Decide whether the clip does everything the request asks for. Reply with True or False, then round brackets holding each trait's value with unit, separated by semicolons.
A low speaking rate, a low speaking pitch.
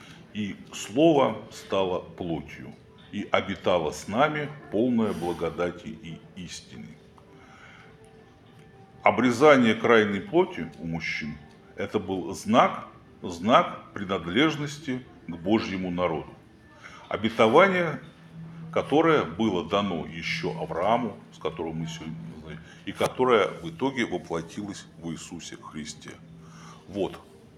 True (100 wpm; 100 Hz)